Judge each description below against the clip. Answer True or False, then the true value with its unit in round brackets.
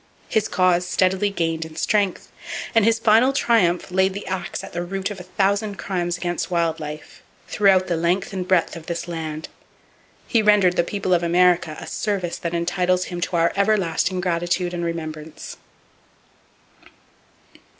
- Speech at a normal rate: True (160 wpm)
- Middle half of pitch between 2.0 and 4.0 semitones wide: True (2.5 semitones)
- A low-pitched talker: False (180 Hz)